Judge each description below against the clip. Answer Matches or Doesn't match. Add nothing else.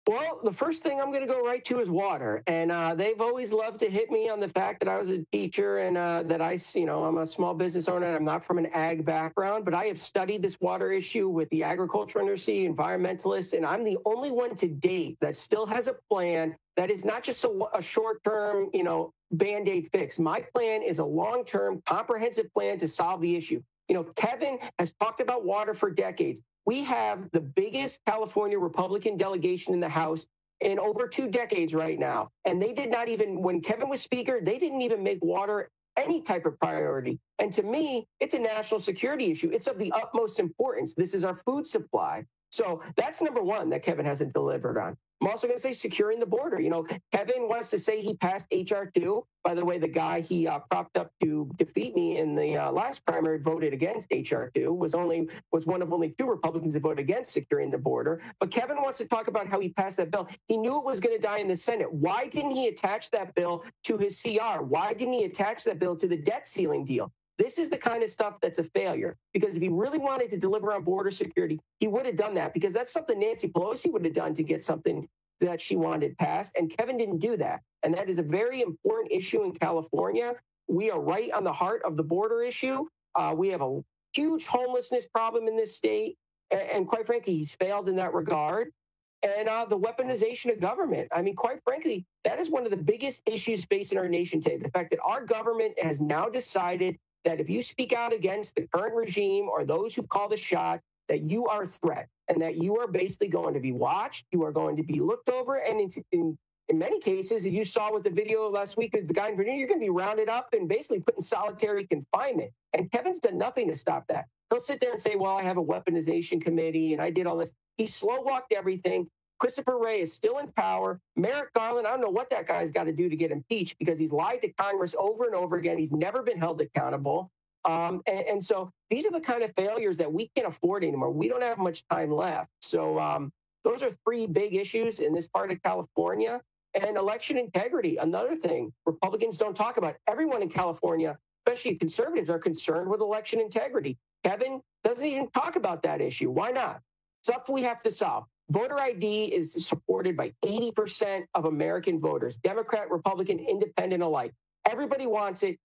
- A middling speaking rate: Doesn't match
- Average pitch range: Doesn't match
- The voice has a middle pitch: Doesn't match